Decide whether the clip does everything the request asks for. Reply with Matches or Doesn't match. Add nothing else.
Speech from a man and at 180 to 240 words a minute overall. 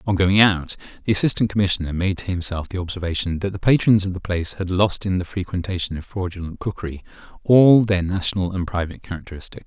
Matches